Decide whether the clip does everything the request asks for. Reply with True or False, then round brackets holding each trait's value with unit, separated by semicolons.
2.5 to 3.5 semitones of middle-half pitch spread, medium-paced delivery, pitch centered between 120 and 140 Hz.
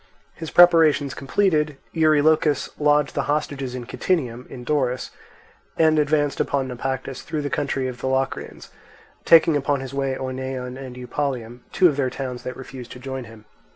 True (2.8 semitones; 160 wpm; 135 Hz)